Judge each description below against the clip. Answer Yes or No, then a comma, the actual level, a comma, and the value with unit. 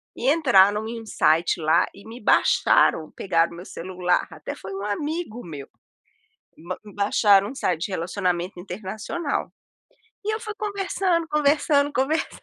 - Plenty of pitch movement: Yes, wide, 8.3 semitones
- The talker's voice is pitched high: Yes, high, 205 Hz